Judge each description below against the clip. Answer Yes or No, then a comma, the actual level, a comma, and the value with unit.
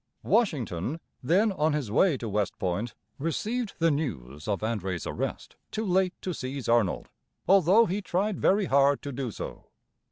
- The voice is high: No, medium, 145 Hz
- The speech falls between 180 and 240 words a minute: No, average, 160 wpm